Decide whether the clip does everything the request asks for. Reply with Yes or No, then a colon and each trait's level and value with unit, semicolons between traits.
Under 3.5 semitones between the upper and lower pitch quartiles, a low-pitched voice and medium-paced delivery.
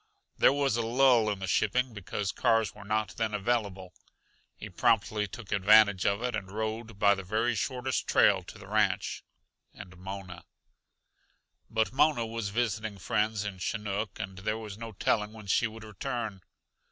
Yes: narrow, 2.4 semitones; low, 110 Hz; average, 165 wpm